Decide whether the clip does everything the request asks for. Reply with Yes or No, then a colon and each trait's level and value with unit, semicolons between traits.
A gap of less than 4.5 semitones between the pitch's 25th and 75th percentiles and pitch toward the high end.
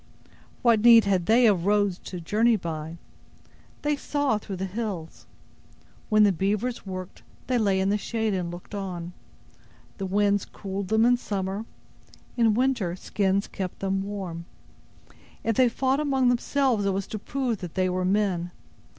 Yes: average, 3.6 semitones; high, 200 Hz